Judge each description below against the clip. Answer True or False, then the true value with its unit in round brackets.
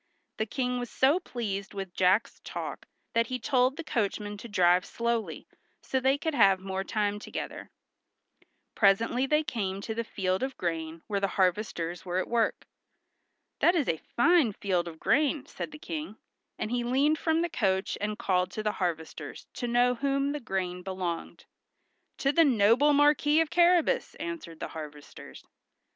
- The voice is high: True (225 Hz)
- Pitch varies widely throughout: True (6.4 semitones)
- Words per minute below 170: False (175 wpm)